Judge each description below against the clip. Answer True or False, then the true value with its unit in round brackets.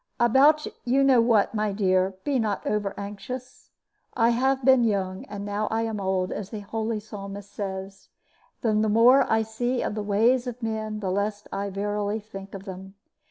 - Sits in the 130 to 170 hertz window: False (215 Hz)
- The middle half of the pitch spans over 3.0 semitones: False (2.7 semitones)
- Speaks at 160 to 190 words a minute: True (175 wpm)